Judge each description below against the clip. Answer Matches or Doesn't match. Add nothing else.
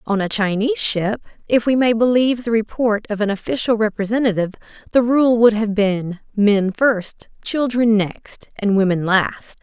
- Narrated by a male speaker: Doesn't match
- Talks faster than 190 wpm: Doesn't match